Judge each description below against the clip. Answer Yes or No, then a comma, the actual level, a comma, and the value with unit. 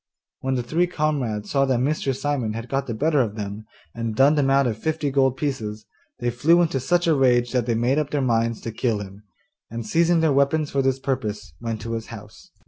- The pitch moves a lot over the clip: No, average, 4.1 semitones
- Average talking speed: No, fast, 225 wpm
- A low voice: Yes, low, 130 Hz